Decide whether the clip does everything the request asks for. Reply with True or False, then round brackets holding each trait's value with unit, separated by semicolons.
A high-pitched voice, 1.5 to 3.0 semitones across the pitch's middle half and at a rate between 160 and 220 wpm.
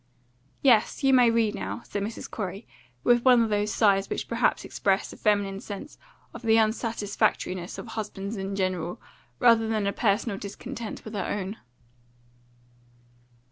False (210 Hz; 2.6 semitones; 150 wpm)